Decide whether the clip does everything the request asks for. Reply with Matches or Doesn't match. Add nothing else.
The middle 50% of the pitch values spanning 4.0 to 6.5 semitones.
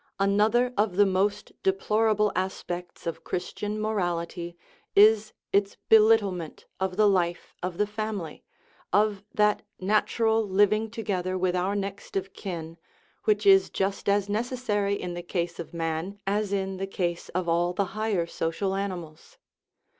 Doesn't match